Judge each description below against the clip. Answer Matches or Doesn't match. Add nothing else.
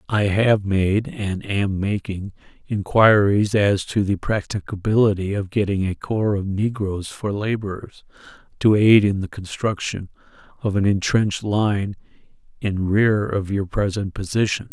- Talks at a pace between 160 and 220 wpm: Doesn't match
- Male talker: Matches